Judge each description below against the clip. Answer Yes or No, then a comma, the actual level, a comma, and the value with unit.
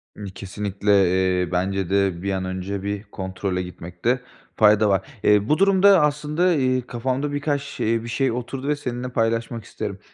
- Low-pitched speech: Yes, low, 110 Hz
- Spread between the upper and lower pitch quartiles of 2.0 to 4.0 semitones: No, wide, 5.5 semitones